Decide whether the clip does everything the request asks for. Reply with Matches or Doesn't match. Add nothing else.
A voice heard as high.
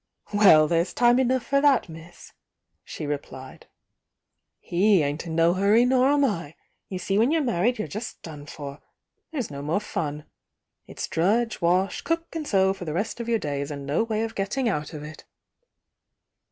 Matches